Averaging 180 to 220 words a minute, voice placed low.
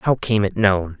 No: fast, 240 wpm; low, 100 Hz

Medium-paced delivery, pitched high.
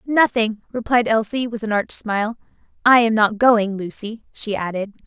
Yes: average, 165 wpm; high, 220 Hz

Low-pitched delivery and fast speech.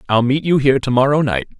Yes: low, 130 Hz; fast, 265 wpm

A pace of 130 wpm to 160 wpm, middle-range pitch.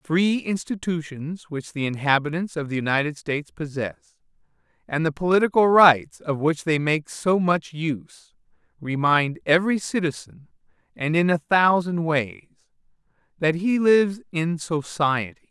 Yes: slow, 135 wpm; medium, 160 Hz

